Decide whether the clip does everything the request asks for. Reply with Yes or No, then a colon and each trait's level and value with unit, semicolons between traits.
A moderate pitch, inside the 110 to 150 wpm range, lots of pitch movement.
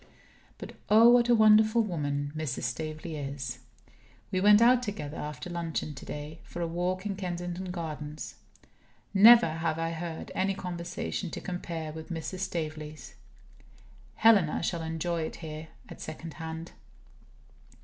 No: medium, 165 Hz; average, 140 wpm; average, 3.4 semitones